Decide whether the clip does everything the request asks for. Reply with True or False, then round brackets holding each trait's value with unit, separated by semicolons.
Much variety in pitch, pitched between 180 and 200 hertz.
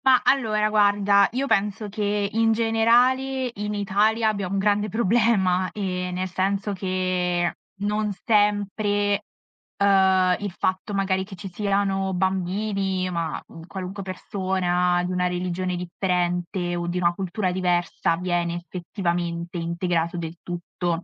False (2.5 semitones; 190 Hz)